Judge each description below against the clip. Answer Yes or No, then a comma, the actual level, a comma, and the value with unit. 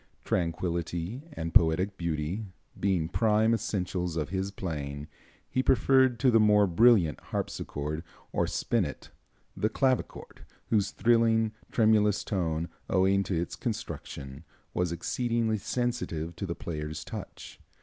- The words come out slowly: Yes, slow, 120 wpm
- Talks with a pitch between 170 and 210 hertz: No, very low, 95 Hz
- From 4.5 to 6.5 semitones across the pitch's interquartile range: Yes, average, 5.1 semitones